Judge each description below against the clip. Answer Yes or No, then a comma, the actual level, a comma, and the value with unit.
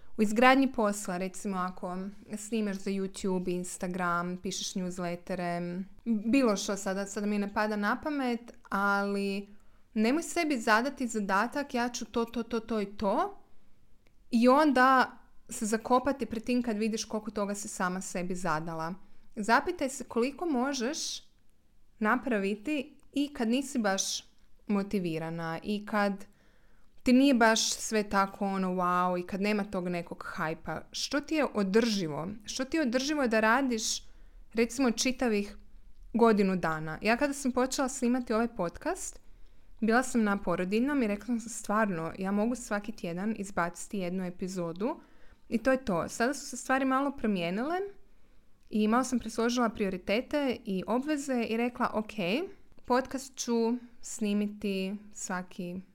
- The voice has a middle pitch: No, high, 220 Hz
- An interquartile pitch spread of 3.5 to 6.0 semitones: Yes, average, 4.2 semitones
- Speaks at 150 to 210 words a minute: No, average, 140 wpm